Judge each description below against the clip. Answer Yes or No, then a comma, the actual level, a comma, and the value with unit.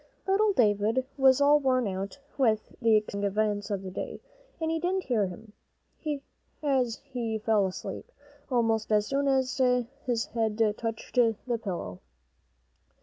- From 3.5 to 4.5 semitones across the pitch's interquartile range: Yes, average, 4.0 semitones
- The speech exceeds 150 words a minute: No, average, 145 wpm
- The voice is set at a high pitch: Yes, high, 225 Hz